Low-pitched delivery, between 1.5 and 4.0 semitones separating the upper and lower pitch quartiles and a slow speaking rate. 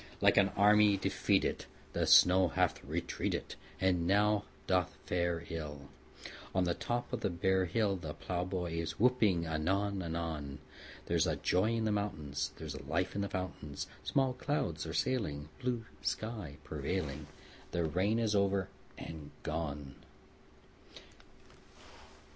No: very low, 90 Hz; average, 4.4 semitones; slow, 130 wpm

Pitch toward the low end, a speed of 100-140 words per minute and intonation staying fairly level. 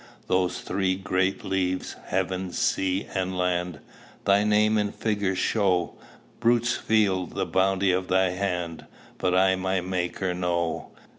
Yes: very low, 95 Hz; slow, 135 wpm; narrow, 1.3 semitones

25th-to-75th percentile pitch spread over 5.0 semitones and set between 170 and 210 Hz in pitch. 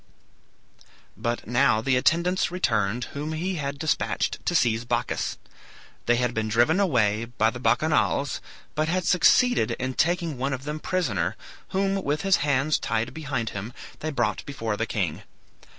No: wide, 5.6 semitones; low, 135 Hz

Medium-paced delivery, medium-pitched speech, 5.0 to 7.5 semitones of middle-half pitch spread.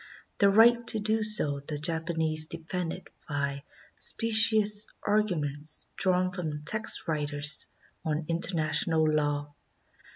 No: slow, 105 wpm; medium, 165 Hz; wide, 5.6 semitones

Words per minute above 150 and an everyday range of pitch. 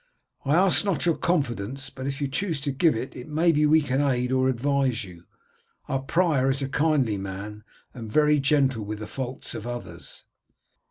Yes: average, 180 wpm; average, 3.6 semitones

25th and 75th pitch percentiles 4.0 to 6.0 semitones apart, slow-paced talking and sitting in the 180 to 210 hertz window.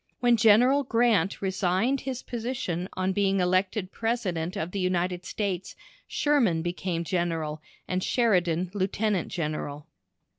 Yes: average, 4.3 semitones; slow, 120 wpm; medium, 185 Hz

